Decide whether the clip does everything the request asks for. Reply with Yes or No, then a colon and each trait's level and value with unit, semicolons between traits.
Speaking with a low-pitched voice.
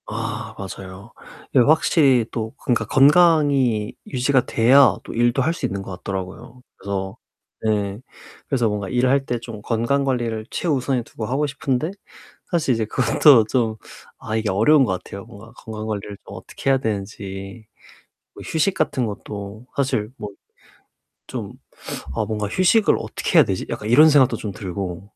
Yes: low, 115 Hz